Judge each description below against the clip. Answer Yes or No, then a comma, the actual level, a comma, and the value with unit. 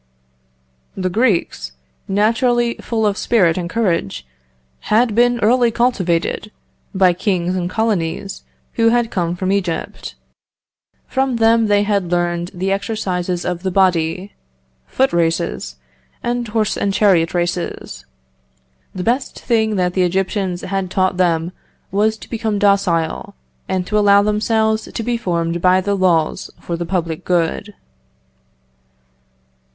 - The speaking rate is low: Yes, slow, 130 wpm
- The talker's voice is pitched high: Yes, high, 195 Hz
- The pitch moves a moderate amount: Yes, average, 3.9 semitones